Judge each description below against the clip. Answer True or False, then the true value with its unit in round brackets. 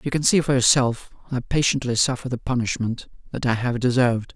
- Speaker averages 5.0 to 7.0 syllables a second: True (5.8 syllables/s)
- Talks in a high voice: False (125 Hz)